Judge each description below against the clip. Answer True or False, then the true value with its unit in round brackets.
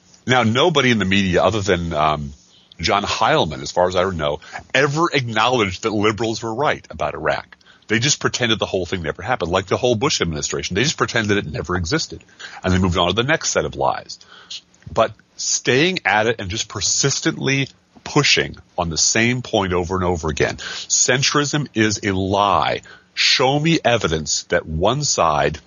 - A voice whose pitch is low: True (105 Hz)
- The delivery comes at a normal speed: True (180 wpm)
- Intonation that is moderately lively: False (5.7 semitones)